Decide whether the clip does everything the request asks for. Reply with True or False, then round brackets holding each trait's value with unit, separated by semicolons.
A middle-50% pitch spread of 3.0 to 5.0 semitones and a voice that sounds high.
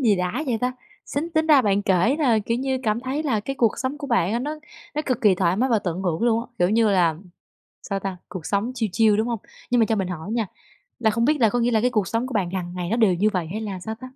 True (4.3 semitones; 220 Hz)